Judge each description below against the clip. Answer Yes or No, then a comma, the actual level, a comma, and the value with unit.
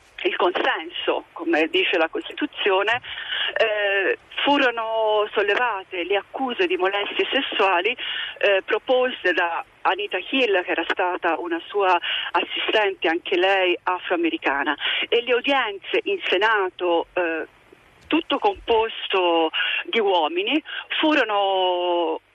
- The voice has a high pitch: Yes, high, 205 Hz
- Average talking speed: No, slow, 105 wpm